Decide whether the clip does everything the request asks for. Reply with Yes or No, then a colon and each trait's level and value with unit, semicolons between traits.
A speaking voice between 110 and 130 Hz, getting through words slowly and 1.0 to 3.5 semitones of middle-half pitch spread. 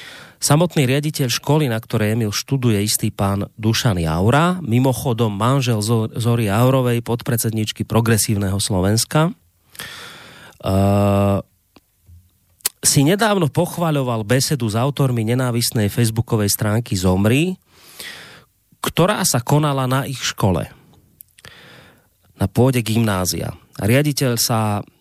No: low, 115 Hz; slow, 100 wpm; average, 4.7 semitones